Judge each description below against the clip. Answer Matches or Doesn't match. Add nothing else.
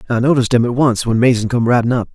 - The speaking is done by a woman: Doesn't match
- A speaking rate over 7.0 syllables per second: Matches